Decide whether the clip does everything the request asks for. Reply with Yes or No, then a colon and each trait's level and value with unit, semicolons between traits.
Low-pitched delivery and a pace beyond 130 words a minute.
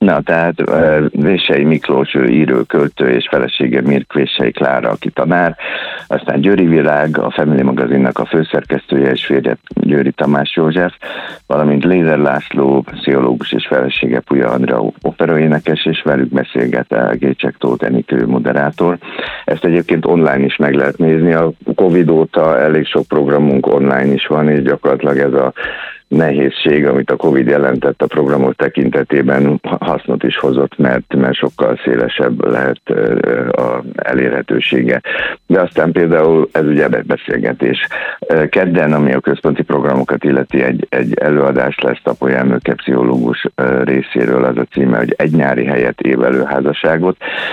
Yes: very low, 70 Hz; average, 140 wpm